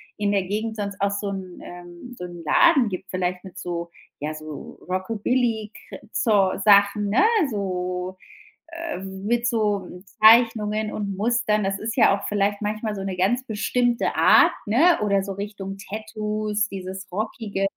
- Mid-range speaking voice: No, high, 205 Hz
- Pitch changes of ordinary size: No, narrow, 2.3 semitones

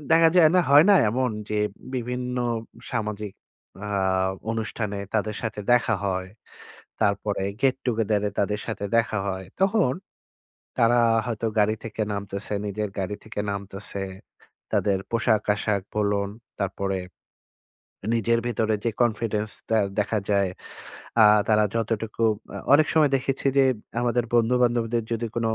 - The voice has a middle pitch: No, low, 110 Hz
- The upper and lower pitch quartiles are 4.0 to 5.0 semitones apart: No, average, 2.7 semitones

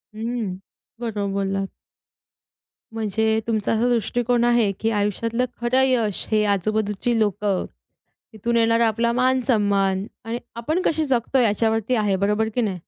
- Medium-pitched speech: No, high, 220 Hz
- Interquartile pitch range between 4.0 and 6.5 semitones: No, narrow, 2.6 semitones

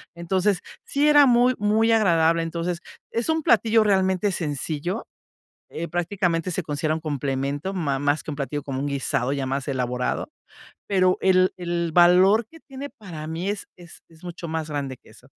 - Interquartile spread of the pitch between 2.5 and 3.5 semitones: No, average, 5.1 semitones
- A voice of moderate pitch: Yes, medium, 170 Hz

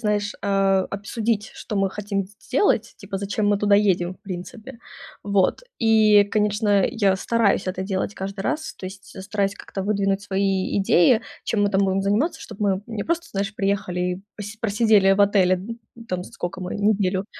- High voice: Yes, high, 200 Hz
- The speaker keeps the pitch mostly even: Yes, narrow, 1.6 semitones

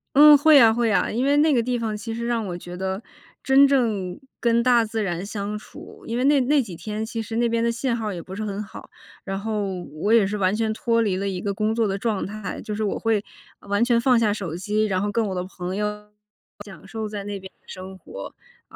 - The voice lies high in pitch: Yes, high, 215 Hz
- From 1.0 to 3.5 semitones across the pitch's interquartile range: Yes, average, 2.9 semitones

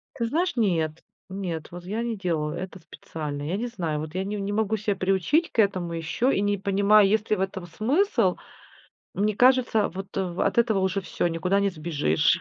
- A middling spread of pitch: Yes, average, 3.8 semitones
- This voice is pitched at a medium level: No, high, 195 Hz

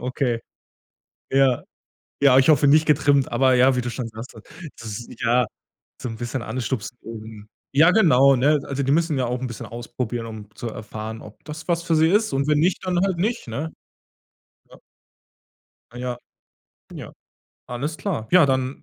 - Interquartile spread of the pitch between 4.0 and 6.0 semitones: Yes, average, 4.3 semitones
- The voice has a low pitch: Yes, low, 130 Hz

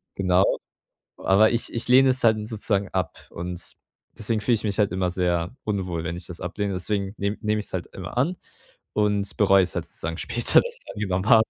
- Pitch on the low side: Yes, low, 100 Hz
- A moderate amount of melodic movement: Yes, average, 3.2 semitones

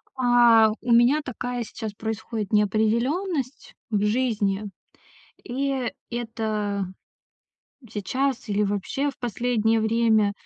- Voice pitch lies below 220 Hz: No, high, 225 Hz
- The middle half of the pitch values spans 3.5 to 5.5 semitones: No, average, 2.8 semitones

